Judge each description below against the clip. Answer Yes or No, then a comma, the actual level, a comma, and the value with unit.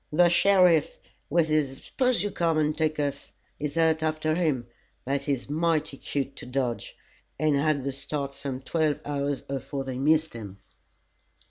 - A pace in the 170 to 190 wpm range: No, average, 160 wpm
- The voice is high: No, medium, 150 Hz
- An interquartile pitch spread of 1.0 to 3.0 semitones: Yes, narrow, 2.5 semitones